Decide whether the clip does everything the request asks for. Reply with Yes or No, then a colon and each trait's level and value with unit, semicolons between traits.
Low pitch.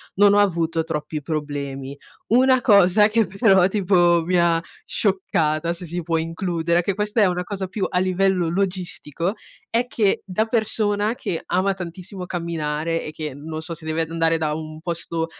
No: medium, 175 Hz